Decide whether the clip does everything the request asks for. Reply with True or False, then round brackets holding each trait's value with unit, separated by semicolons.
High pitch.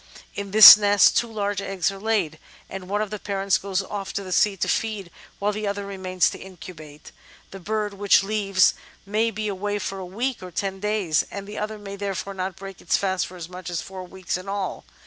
True (195 Hz)